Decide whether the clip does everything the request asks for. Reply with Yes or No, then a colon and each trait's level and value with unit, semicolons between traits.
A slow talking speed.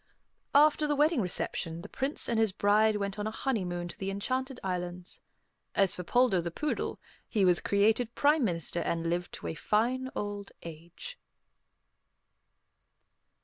No: average, 150 wpm